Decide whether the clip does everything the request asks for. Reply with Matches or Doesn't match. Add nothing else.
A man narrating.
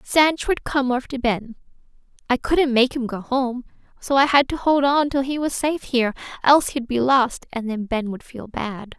Doesn't match